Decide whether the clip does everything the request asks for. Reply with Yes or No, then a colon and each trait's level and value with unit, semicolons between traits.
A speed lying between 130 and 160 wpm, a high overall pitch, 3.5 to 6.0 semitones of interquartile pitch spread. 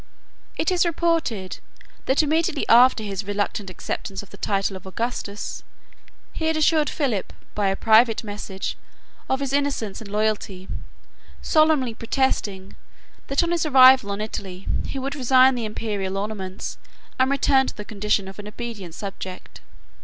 Yes: average, 150 wpm; high, 220 Hz; average, 5.3 semitones